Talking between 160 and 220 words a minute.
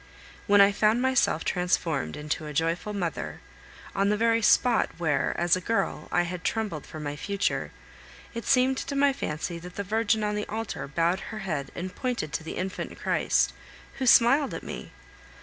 Yes: average, 185 wpm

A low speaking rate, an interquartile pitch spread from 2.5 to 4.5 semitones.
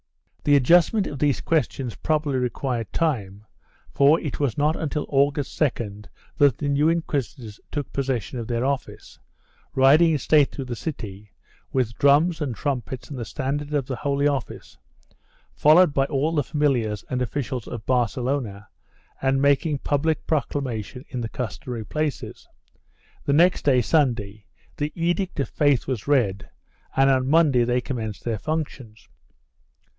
No: average, 155 wpm; average, 3.5 semitones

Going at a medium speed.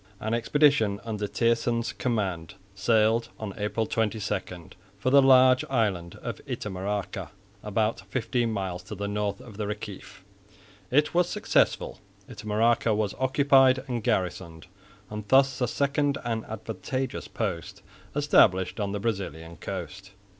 No: slow, 130 wpm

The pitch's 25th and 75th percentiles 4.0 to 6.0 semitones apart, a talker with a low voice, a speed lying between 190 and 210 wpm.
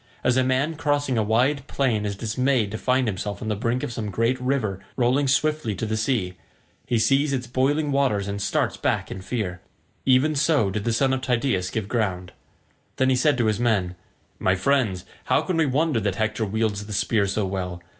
Yes: average, 4.5 semitones; low, 115 Hz; average, 200 wpm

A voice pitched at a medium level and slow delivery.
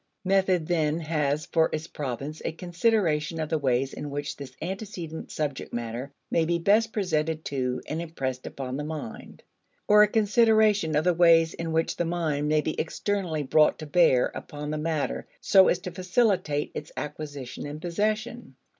No: medium, 160 Hz; average, 170 wpm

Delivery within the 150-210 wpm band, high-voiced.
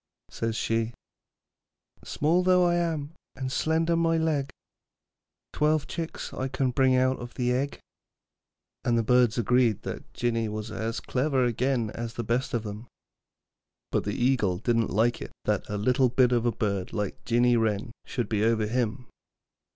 No: average, 165 wpm; low, 120 Hz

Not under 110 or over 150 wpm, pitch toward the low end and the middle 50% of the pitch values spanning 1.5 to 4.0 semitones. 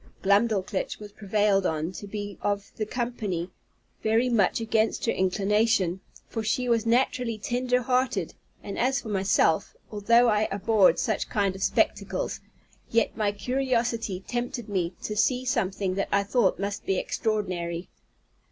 No: average, 145 wpm; high, 210 Hz; average, 3.2 semitones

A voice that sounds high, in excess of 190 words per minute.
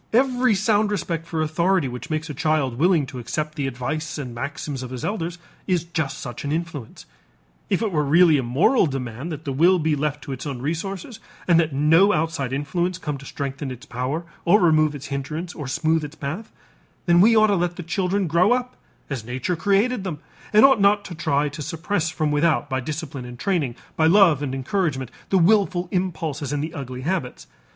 No: medium, 155 Hz; fast, 205 wpm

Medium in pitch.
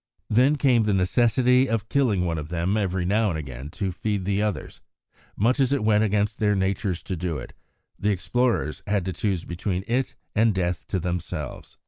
No: low, 100 Hz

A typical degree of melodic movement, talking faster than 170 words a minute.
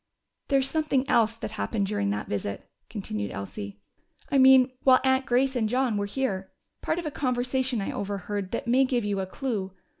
Yes: average, 5.0 semitones; average, 185 wpm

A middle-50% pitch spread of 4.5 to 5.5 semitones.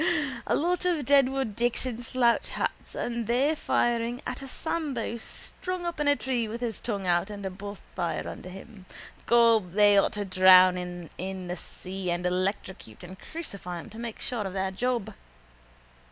Yes: average, 5.0 semitones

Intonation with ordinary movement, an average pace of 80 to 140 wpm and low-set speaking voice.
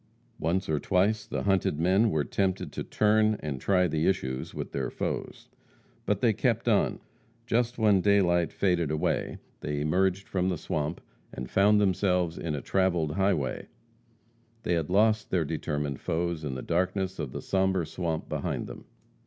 No: average, 4.0 semitones; average, 165 wpm; very low, 90 Hz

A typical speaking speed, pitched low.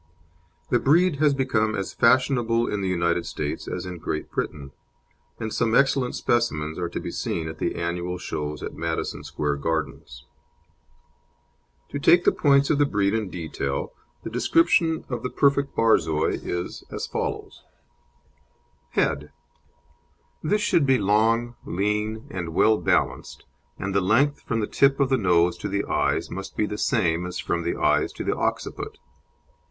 Yes: average, 160 wpm; low, 105 Hz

